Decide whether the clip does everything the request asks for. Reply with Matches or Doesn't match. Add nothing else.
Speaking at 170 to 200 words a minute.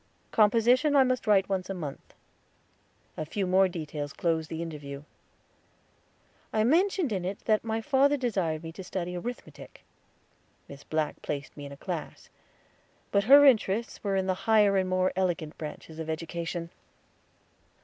Doesn't match